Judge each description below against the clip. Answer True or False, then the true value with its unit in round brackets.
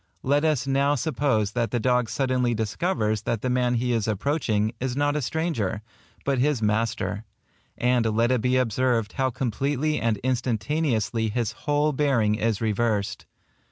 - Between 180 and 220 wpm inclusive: False (160 wpm)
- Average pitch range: True (3.8 semitones)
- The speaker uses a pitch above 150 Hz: False (125 Hz)